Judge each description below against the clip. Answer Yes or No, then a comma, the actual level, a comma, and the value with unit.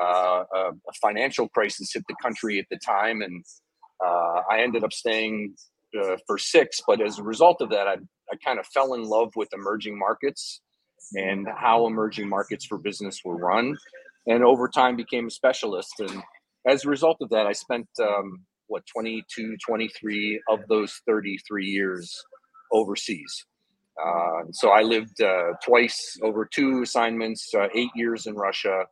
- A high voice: No, low, 110 Hz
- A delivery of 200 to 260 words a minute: No, average, 165 wpm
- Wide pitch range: No, average, 4.1 semitones